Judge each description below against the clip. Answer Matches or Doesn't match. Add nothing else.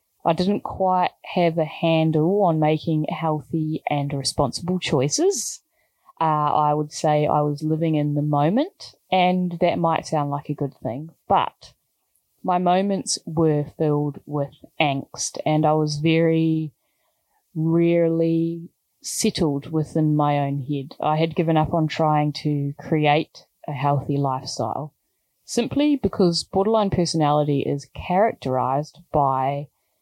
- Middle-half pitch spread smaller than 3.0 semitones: Matches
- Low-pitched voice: Doesn't match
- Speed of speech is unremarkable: Doesn't match